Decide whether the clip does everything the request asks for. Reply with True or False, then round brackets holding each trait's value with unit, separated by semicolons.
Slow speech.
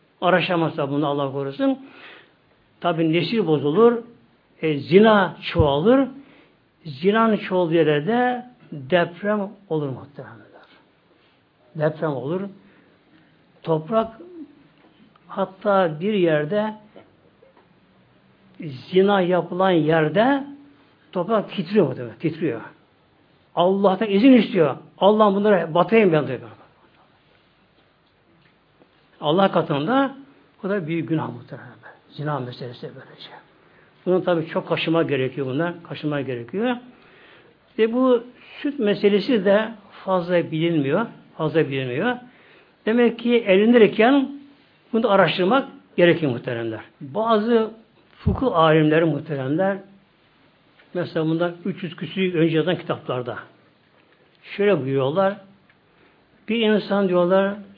True (90 wpm)